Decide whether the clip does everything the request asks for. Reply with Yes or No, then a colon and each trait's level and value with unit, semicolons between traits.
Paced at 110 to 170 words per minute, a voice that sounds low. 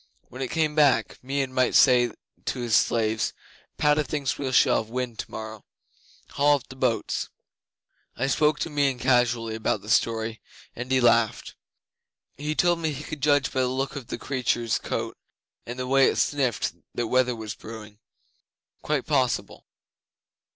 Yes: average, 165 wpm; low, 130 Hz